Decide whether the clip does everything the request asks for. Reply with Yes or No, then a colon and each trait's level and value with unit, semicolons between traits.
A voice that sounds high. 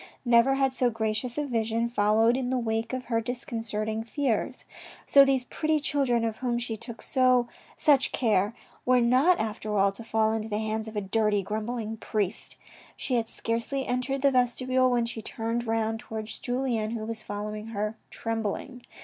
Yes: high, 230 Hz